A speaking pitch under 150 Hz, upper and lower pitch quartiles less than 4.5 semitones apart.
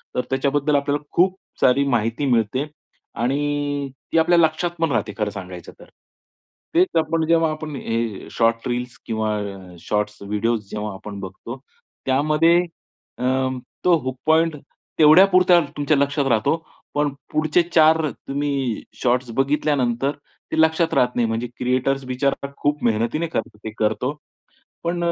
No: low, 135 Hz; wide, 5.4 semitones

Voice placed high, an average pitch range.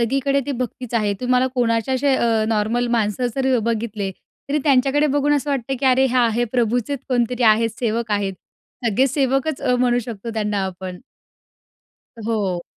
Yes: high, 245 Hz; average, 3.3 semitones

